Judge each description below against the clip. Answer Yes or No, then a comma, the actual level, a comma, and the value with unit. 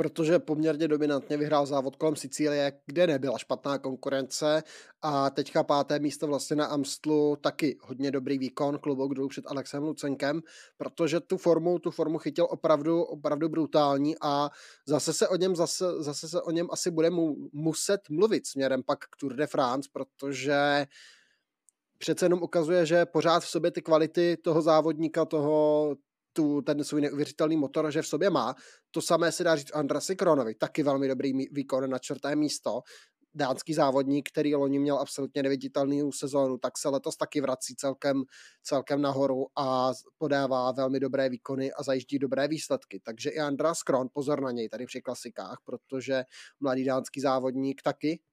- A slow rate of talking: No, average, 165 wpm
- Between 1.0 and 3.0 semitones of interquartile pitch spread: Yes, narrow, 2.5 semitones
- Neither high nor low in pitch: Yes, medium, 145 Hz